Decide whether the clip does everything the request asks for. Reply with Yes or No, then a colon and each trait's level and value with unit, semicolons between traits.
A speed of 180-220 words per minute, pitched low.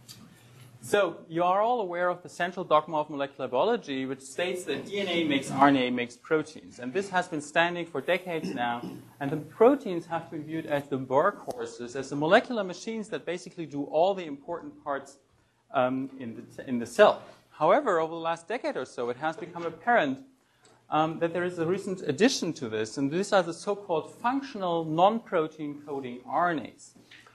No: average, 185 wpm; medium, 160 Hz